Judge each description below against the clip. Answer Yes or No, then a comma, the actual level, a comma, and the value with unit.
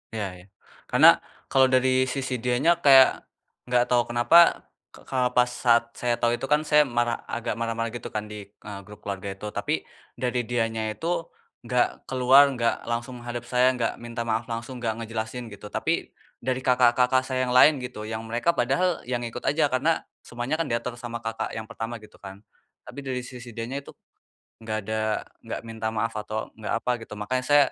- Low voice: Yes, low, 120 Hz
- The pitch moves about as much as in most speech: No, narrow, 2.3 semitones